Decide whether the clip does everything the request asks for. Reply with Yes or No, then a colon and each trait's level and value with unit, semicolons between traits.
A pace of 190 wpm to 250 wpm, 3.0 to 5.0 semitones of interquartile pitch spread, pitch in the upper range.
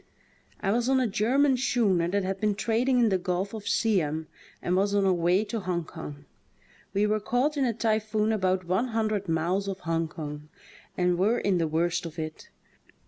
Yes: average, 195 wpm; average, 4.1 semitones; high, 195 Hz